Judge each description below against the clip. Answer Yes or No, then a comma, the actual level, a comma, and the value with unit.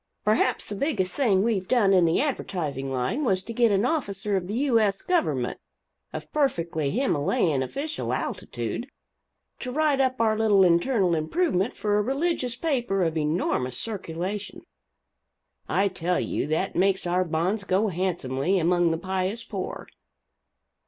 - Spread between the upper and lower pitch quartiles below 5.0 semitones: No, wide, 5.4 semitones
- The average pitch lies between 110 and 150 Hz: No, high, 195 Hz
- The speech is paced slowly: No, average, 150 wpm